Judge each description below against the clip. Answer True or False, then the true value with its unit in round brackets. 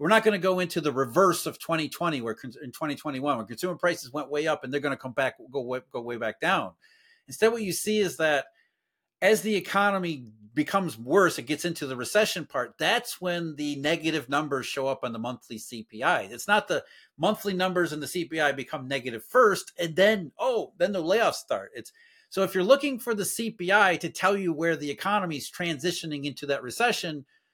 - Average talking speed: False (210 wpm)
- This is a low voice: False (165 Hz)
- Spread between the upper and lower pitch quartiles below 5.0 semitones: False (5.5 semitones)